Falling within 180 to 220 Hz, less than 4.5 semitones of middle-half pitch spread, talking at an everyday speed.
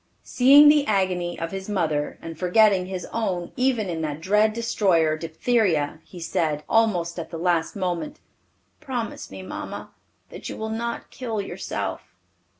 No: medium, 185 Hz; average, 5.2 semitones; average, 150 wpm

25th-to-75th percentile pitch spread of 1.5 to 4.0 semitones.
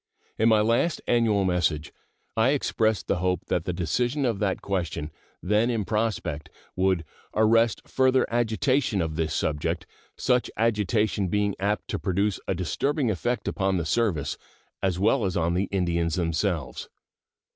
No: average, 4.5 semitones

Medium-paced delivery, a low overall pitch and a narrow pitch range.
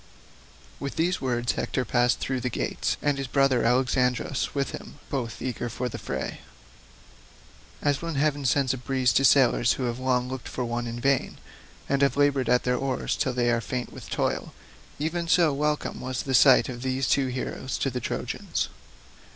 Yes: average, 185 wpm; low, 130 Hz; narrow, 2.0 semitones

